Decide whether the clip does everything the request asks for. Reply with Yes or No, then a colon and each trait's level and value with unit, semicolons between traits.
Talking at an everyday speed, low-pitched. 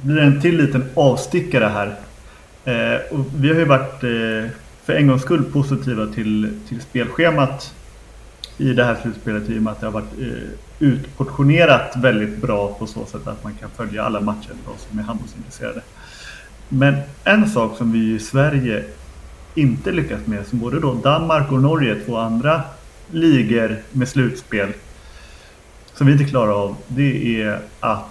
Yes: average, 165 wpm; low, 120 Hz